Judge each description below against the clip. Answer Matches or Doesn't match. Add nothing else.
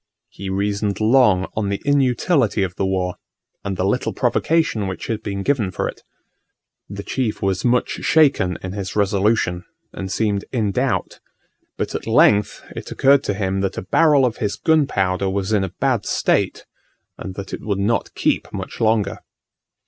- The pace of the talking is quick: Doesn't match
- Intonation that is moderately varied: Matches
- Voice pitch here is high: Doesn't match